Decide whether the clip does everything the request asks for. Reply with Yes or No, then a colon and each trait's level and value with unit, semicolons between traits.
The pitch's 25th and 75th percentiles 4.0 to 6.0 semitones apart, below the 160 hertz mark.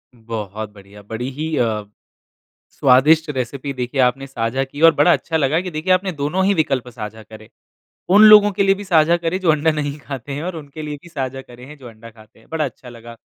Yes: average, 5.2 semitones; medium, 140 Hz